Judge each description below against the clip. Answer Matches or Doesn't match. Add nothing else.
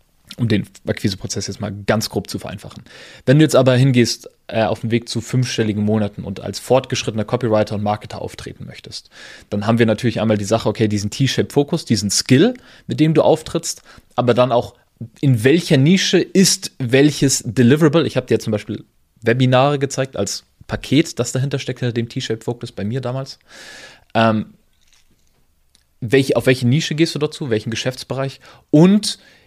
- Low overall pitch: Matches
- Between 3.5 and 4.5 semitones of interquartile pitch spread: Matches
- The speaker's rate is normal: Matches